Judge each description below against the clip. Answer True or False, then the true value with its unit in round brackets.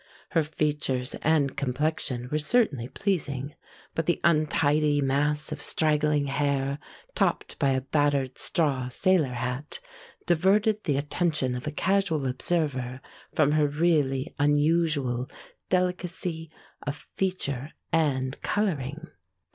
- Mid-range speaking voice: True (150 Hz)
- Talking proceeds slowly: True (115 wpm)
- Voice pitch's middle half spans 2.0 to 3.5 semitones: True (3.1 semitones)